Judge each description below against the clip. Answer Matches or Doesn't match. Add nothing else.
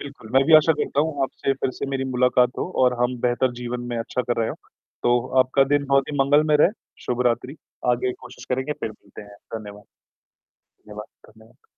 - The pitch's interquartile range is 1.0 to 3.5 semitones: Matches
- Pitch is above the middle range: Doesn't match